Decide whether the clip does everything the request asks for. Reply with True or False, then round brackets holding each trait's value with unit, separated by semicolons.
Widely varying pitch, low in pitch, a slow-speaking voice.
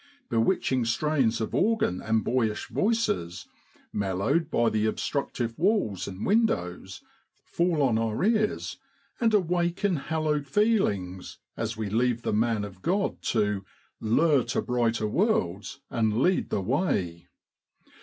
True (8.5 semitones; 120 Hz; 130 wpm)